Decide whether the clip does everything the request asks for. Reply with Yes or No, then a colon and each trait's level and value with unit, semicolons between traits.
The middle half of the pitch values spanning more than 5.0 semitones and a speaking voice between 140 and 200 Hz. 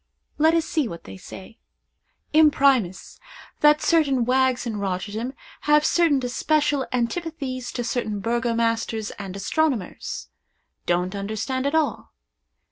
No: wide, 5.6 semitones; very high, 250 Hz